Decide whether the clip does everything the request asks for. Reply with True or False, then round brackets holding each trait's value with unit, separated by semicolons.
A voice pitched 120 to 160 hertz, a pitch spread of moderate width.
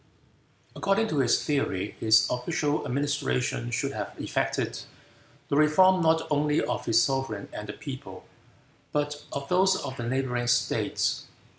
True (140 Hz; 4.3 semitones)